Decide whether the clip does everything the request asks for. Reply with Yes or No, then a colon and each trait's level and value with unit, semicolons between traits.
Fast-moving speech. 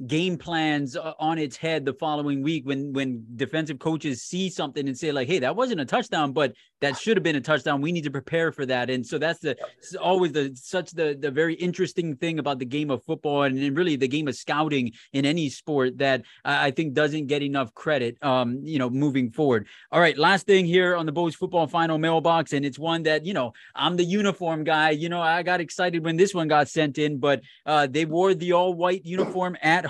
Yes: fast, 235 wpm